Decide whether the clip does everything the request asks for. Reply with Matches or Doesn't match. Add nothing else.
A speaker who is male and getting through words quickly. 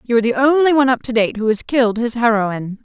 Doesn't match